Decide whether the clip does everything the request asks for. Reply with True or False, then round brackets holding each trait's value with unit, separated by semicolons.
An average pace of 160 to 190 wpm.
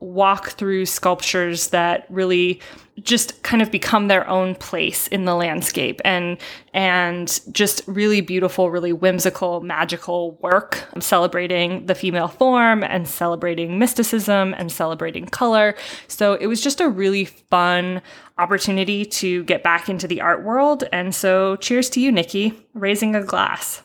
False (150 wpm)